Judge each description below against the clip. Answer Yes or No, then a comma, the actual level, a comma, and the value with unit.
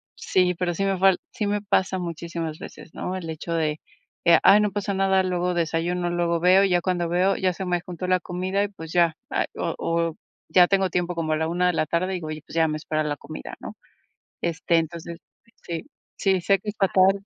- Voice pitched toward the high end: No, medium, 175 Hz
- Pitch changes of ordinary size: No, narrow, 2.2 semitones